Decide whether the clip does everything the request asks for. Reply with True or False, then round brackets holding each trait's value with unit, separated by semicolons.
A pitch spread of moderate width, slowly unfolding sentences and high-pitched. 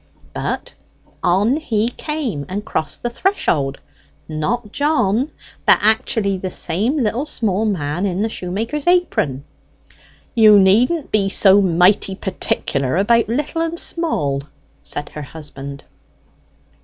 False (5.7 semitones; 125 wpm; 205 Hz)